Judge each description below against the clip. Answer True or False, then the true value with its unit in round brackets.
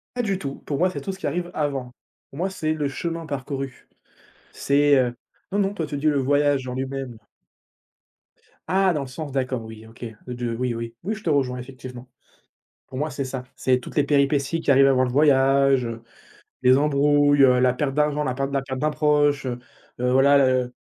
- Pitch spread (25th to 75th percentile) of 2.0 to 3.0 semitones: True (2.6 semitones)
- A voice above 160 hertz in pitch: False (140 Hz)